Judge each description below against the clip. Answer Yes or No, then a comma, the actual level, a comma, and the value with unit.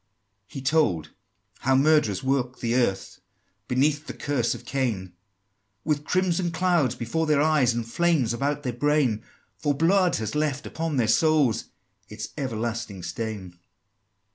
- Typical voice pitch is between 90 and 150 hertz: Yes, low, 135 Hz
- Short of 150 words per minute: Yes, average, 140 wpm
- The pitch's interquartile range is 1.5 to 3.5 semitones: No, average, 4.9 semitones